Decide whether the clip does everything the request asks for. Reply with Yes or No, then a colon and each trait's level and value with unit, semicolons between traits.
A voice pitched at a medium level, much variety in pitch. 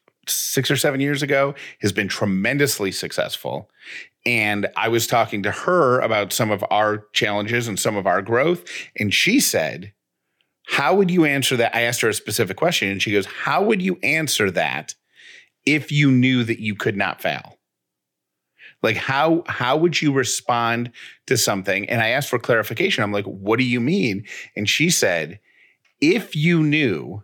No: low, 125 Hz; wide, 6.1 semitones